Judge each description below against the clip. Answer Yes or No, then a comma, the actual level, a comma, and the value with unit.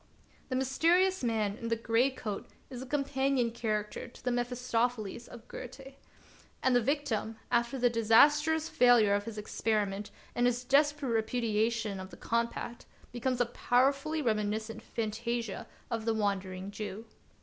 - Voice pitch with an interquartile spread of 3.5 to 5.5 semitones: No, average, 3.0 semitones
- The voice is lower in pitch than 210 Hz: No, high, 235 Hz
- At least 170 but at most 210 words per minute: No, average, 145 wpm